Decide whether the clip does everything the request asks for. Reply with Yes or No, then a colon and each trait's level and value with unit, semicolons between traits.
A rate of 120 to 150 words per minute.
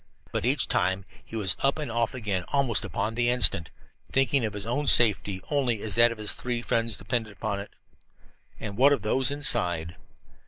No: average, 190 wpm